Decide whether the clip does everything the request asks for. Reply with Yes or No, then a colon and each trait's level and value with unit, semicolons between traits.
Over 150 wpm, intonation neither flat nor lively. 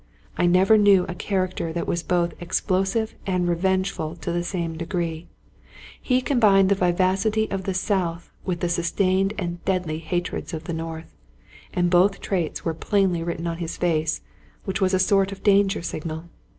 No: average, 170 wpm; narrow, 2.3 semitones